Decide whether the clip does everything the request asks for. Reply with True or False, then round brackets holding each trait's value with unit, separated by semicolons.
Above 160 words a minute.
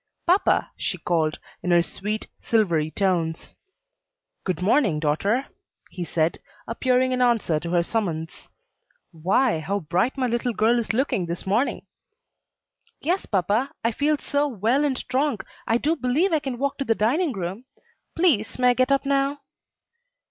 False (155 wpm)